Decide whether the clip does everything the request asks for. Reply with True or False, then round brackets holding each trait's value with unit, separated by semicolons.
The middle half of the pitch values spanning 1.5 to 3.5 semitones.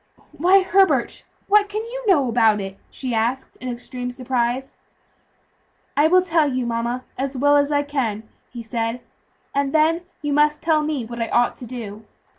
False (4.5 semitones)